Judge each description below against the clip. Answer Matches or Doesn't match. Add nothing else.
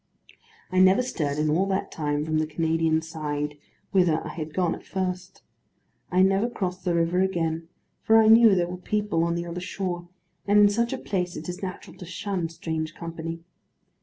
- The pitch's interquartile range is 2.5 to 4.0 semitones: Matches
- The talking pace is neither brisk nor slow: Matches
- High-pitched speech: Doesn't match